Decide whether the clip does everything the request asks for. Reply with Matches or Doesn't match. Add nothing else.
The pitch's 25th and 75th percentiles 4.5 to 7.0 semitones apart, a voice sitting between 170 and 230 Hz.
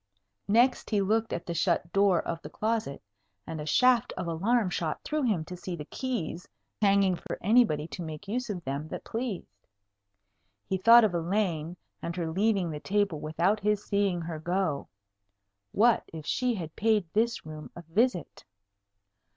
Matches